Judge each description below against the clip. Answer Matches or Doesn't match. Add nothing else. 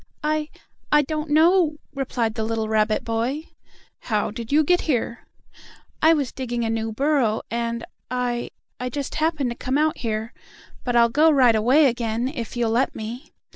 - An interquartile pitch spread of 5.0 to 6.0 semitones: Doesn't match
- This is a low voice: Doesn't match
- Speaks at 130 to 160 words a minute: Doesn't match